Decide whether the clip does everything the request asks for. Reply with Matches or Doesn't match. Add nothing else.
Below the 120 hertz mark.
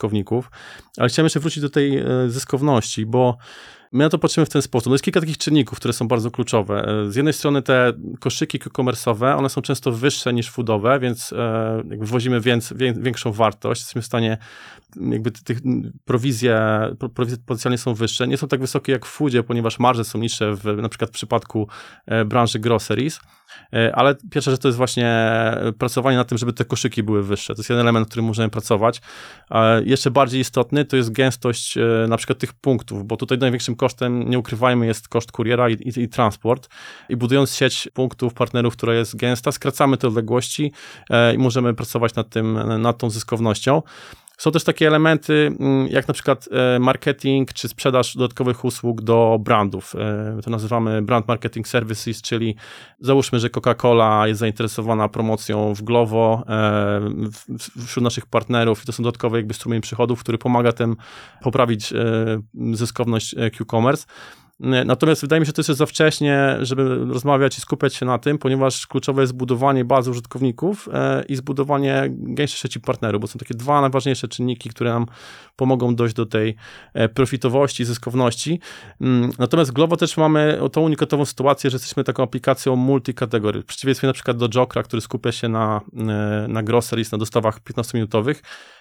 Doesn't match